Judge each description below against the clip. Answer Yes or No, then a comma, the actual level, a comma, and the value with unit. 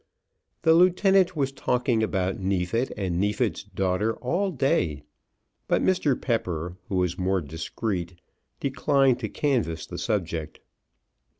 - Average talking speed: No, slow, 120 wpm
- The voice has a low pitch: Yes, low, 105 Hz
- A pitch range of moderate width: No, wide, 7.2 semitones